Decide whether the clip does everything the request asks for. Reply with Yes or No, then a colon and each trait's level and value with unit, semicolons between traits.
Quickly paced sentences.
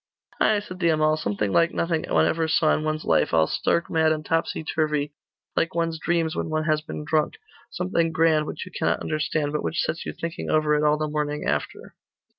Yes: fast, 215 wpm